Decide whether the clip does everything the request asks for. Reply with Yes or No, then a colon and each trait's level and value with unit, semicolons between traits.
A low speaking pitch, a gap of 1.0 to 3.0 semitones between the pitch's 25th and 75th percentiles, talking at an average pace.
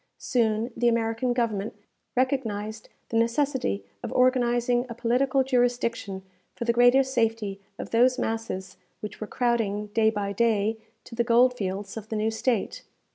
No: high, 230 Hz; narrow, 2.4 semitones; average, 150 wpm